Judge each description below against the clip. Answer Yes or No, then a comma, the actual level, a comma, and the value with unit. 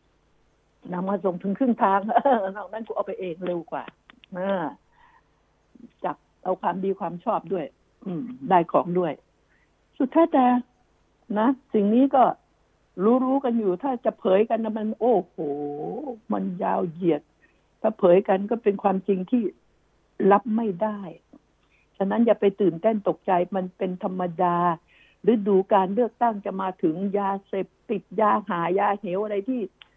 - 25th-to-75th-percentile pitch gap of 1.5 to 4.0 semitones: Yes, average, 3.3 semitones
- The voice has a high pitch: Yes, high, 200 Hz